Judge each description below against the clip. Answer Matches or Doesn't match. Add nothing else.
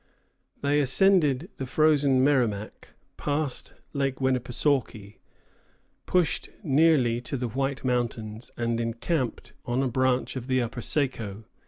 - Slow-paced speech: Matches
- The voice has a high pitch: Doesn't match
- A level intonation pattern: Doesn't match